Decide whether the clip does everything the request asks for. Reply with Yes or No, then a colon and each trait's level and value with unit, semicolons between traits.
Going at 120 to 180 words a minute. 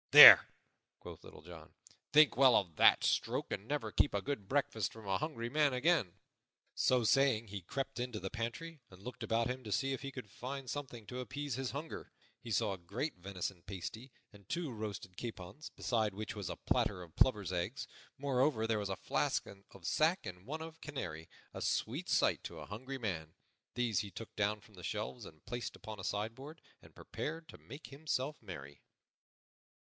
No: average, 190 wpm